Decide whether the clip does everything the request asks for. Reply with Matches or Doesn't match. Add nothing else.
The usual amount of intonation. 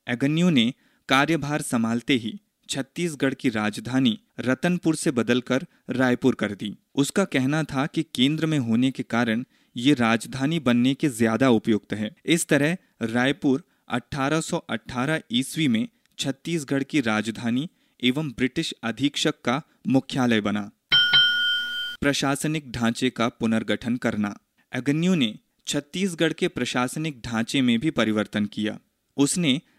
Matches